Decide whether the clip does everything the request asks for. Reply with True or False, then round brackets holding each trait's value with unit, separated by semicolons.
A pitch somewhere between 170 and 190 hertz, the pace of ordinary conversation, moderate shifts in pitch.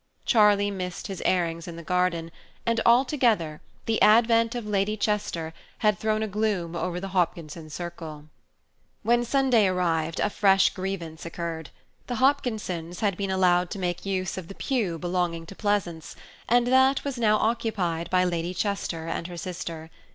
True (185 Hz; 160 wpm; 4.2 semitones)